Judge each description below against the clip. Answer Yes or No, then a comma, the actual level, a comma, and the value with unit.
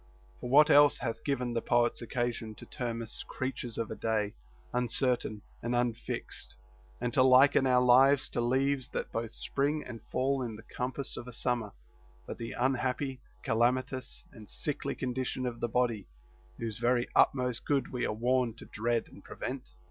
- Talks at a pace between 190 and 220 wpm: No, average, 170 wpm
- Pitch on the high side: No, low, 125 Hz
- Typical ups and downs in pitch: No, narrow, 2.0 semitones